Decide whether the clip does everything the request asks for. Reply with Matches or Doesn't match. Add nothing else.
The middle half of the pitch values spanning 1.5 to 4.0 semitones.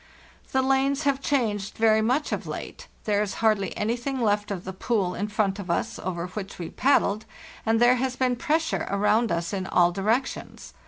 Doesn't match